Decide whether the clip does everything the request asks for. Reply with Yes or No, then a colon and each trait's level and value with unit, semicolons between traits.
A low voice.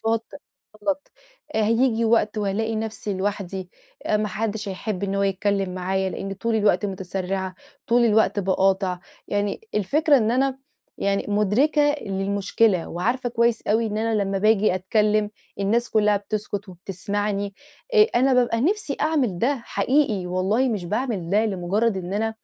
No: high, 210 Hz